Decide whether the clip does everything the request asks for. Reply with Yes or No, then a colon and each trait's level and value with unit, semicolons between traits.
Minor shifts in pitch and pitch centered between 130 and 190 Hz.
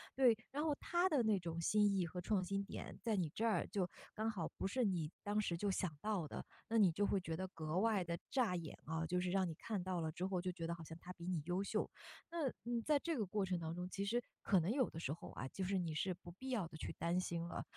No: average, 4.1 semitones; medium, 185 Hz